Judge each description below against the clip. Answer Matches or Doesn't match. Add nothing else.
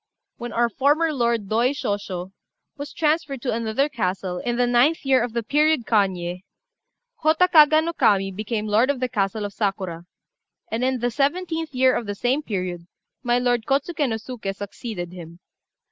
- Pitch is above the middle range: Matches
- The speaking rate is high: Doesn't match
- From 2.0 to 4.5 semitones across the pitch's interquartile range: Doesn't match